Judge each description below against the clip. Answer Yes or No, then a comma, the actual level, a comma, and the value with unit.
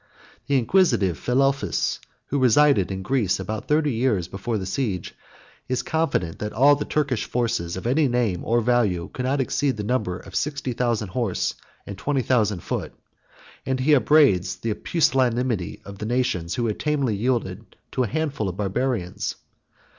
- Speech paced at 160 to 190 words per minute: Yes, average, 165 wpm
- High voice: No, low, 120 Hz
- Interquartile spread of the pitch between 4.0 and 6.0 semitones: Yes, average, 5.1 semitones